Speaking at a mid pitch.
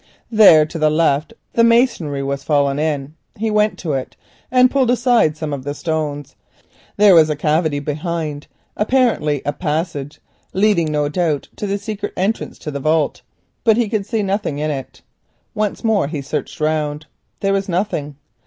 Yes: medium, 160 Hz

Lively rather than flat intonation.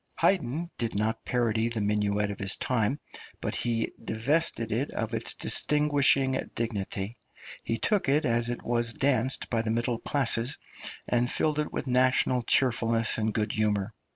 No: average, 3.0 semitones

